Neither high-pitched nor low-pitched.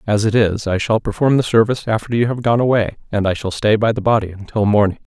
No: low, 110 Hz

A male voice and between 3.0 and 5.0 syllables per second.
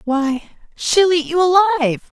No: female; 4.6 syllables/s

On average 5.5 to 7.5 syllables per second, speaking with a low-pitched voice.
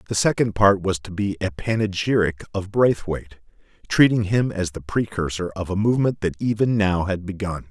No: 5.3 syllables/s; low, 100 Hz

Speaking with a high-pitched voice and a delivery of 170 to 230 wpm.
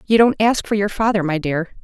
No: high, 200 Hz; fast, 260 wpm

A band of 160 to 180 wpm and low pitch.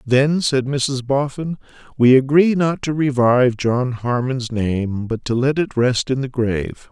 Yes: average, 175 wpm; low, 130 Hz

